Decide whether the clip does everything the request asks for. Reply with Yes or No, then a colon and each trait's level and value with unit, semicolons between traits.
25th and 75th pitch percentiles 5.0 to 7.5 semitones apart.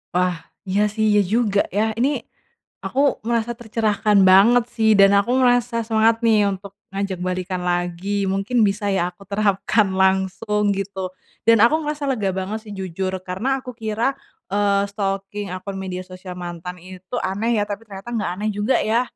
No: average, 2.8 semitones